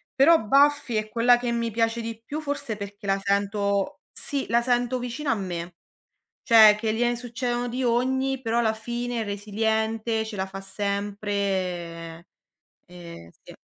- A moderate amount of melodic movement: Yes, average, 3.2 semitones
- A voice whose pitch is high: Yes, high, 220 Hz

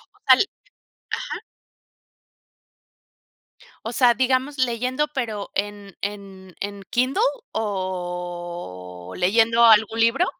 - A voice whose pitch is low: No, high, 205 Hz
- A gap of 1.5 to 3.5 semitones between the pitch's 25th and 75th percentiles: No, average, 4.3 semitones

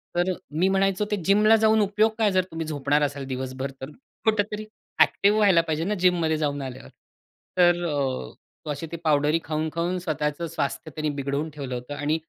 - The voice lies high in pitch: No, medium, 160 Hz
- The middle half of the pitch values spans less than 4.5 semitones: No, average, 5.0 semitones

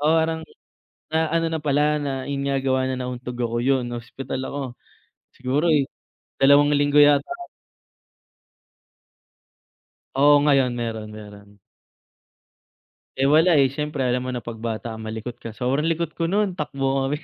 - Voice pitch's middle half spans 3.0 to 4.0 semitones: Yes, average, 3.3 semitones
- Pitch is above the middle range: No, low, 135 Hz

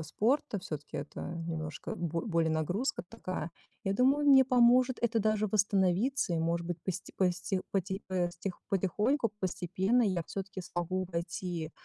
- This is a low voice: No, high, 190 Hz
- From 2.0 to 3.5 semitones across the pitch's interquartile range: No, average, 4.4 semitones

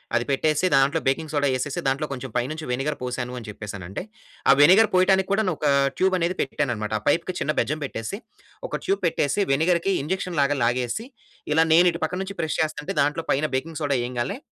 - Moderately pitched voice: Yes, medium, 150 Hz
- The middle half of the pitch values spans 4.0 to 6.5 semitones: Yes, average, 4.7 semitones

